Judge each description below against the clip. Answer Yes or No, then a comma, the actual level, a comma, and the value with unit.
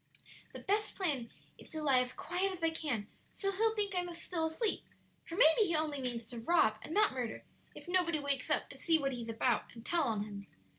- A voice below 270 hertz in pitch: No, very high, 315 Hz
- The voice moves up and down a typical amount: No, wide, 6.5 semitones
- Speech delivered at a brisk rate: Yes, fast, 225 wpm